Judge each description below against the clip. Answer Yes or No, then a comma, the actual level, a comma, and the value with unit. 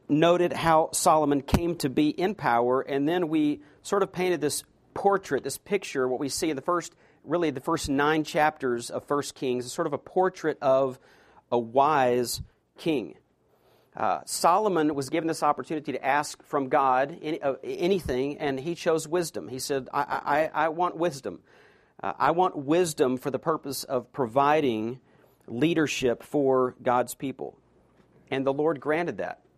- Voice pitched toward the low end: No, medium, 145 Hz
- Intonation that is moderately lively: Yes, average, 3.6 semitones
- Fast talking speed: No, average, 170 wpm